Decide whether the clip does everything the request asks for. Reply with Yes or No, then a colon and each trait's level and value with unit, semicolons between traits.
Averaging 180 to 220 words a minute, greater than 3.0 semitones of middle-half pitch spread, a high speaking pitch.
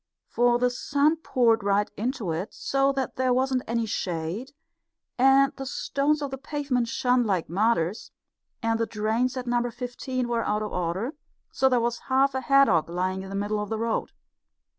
Yes: average, 185 wpm; average, 4.0 semitones; high, 240 Hz